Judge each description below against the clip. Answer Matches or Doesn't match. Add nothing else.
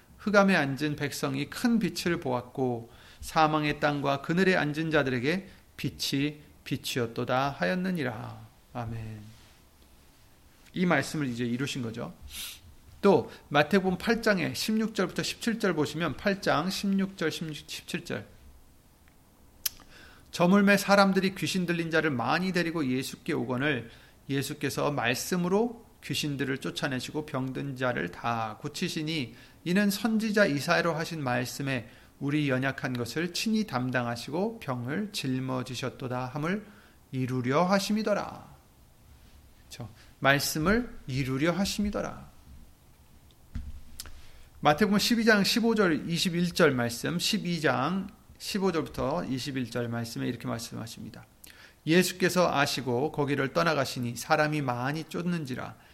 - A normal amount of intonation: Doesn't match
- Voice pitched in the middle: Matches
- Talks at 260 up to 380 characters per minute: Doesn't match